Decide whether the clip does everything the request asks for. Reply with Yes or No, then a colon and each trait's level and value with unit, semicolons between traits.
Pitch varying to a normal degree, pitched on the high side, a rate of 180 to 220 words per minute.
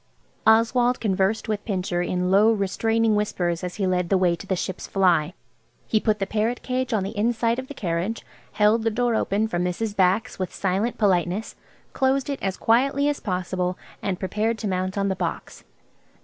Yes: average, 3.6 semitones; high, 205 Hz; average, 190 wpm